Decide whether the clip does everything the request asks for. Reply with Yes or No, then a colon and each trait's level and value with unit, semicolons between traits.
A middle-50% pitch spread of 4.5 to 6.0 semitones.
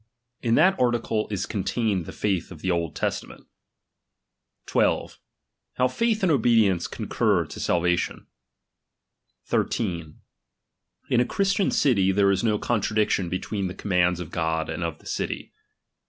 Yes: average, 5.1 semitones